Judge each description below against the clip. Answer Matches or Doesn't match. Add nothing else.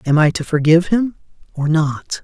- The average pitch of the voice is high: Doesn't match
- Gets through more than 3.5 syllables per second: Matches